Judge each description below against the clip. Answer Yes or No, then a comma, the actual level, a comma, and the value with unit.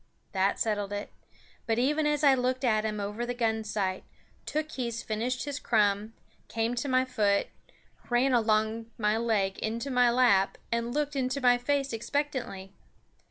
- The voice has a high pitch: Yes, high, 235 Hz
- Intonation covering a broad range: No, average, 3.2 semitones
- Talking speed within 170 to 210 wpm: No, average, 160 wpm